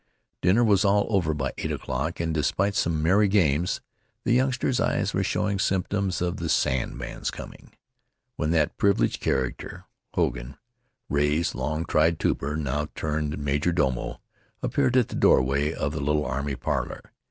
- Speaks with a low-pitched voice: Yes, very low, 80 Hz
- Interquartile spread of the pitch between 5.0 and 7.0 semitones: Yes, wide, 5.4 semitones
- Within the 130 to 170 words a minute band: Yes, average, 155 wpm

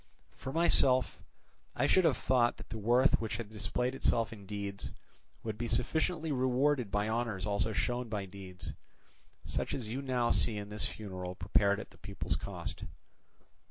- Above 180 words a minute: No, average, 165 wpm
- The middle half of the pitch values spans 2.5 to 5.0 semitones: Yes, average, 3.9 semitones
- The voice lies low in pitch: Yes, low, 115 Hz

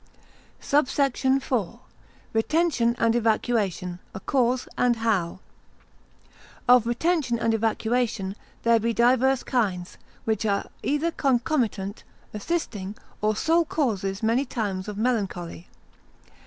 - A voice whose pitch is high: Yes, high, 230 Hz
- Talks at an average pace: No, slow, 100 wpm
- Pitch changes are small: No, average, 3.7 semitones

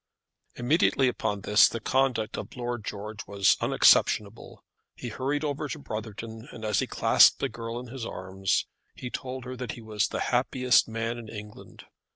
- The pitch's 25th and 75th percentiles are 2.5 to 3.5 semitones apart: Yes, average, 3.0 semitones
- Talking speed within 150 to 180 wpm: Yes, average, 175 wpm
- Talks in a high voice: No, low, 115 Hz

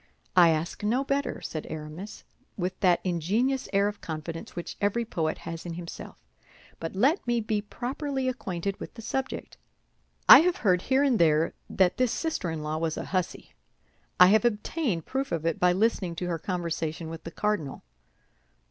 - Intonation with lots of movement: Yes, wide, 6.1 semitones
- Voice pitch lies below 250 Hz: Yes, medium, 185 Hz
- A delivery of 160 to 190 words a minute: Yes, average, 175 wpm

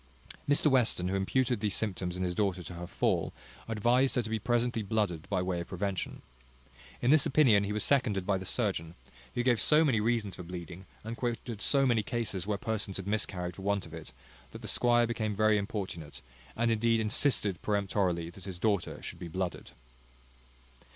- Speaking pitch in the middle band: No, low, 105 Hz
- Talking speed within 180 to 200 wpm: Yes, average, 190 wpm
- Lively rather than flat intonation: No, average, 4.1 semitones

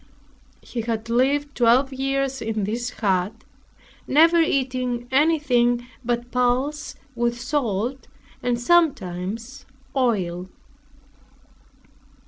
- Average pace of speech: No, slow, 90 wpm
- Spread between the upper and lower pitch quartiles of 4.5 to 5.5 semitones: No, average, 2.9 semitones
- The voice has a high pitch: Yes, high, 245 Hz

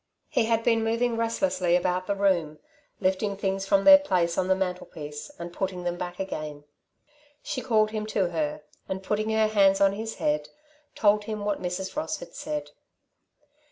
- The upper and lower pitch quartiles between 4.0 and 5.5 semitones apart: No, average, 3.5 semitones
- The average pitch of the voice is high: Yes, high, 195 Hz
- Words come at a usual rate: Yes, average, 175 wpm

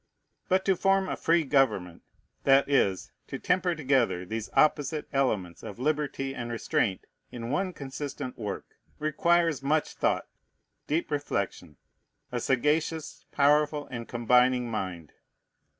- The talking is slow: Yes, slow, 125 wpm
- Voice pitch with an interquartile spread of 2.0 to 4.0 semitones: No, average, 4.6 semitones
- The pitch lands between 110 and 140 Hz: Yes, low, 135 Hz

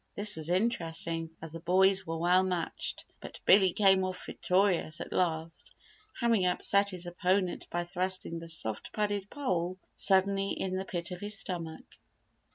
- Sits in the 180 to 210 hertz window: Yes, medium, 185 Hz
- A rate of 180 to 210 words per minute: No, average, 160 wpm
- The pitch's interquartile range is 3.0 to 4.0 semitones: No, narrow, 2.6 semitones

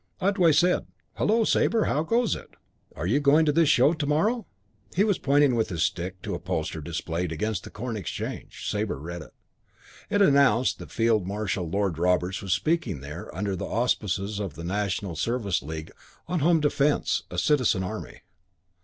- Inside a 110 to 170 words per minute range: No, average, 180 wpm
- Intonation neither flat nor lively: No, wide, 8.8 semitones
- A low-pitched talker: Yes, low, 110 Hz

